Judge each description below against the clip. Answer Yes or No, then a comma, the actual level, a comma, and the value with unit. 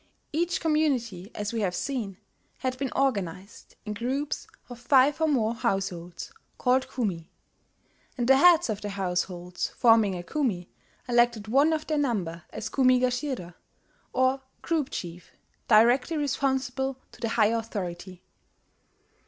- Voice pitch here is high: Yes, high, 240 Hz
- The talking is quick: No, slow, 135 wpm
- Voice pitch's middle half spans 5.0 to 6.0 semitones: Yes, wide, 5.6 semitones